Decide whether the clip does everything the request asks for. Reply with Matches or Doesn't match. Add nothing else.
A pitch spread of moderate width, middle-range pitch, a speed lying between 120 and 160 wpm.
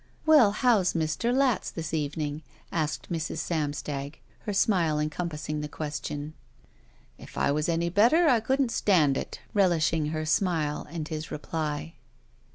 Matches